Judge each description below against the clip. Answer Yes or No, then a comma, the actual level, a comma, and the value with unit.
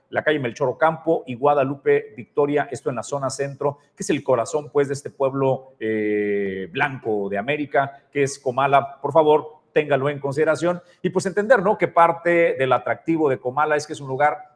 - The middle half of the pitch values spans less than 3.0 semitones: Yes, narrow, 2.6 semitones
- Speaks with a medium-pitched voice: Yes, medium, 145 Hz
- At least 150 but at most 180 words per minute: No, fast, 190 wpm